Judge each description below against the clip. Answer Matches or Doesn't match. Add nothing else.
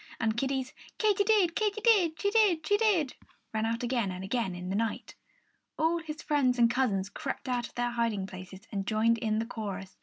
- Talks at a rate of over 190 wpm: Matches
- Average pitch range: Doesn't match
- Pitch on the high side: Matches